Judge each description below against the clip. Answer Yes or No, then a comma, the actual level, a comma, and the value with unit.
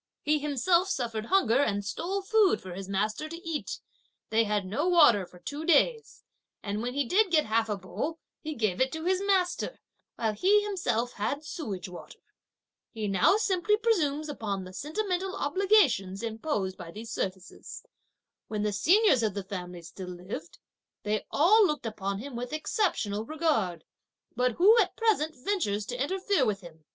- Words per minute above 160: Yes, average, 170 wpm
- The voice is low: No, very high, 250 Hz